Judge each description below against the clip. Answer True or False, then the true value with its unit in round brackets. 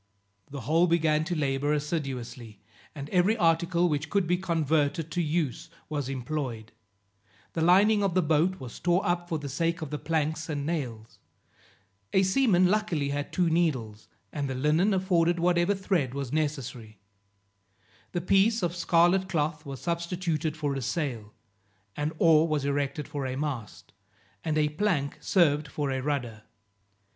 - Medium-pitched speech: True (155 Hz)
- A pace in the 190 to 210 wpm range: False (155 wpm)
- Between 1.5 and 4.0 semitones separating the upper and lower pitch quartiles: True (3.7 semitones)